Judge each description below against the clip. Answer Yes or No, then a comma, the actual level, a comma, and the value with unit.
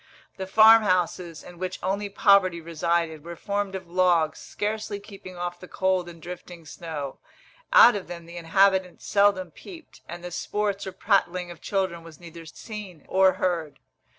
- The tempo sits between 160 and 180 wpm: Yes, average, 165 wpm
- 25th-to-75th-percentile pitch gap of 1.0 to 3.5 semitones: Yes, average, 2.7 semitones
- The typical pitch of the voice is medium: Yes, medium, 180 Hz